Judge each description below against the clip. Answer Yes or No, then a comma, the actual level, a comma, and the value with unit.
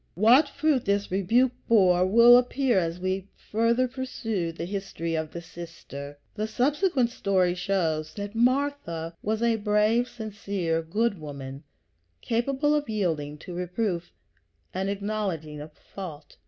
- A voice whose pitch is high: Yes, high, 200 Hz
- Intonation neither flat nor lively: No, wide, 5.7 semitones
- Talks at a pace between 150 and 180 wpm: No, slow, 135 wpm